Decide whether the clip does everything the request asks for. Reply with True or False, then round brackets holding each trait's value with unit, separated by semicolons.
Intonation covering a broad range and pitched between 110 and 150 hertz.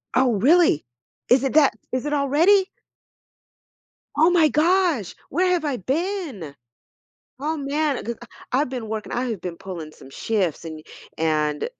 False (8.4 semitones; 265 Hz)